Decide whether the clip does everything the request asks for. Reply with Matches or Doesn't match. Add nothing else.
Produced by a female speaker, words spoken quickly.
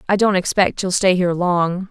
Matches